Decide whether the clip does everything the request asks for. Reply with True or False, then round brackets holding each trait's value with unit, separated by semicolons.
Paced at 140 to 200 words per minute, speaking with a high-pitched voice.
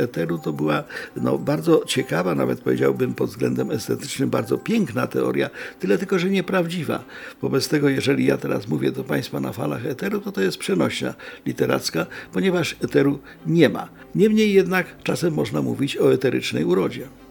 False (160 wpm; 140 Hz)